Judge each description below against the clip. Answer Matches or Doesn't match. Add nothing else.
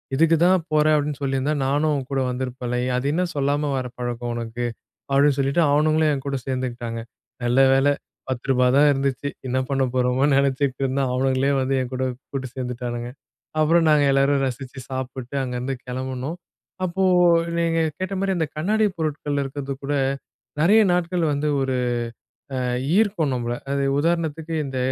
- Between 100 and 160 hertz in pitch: Matches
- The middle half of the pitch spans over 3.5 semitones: Doesn't match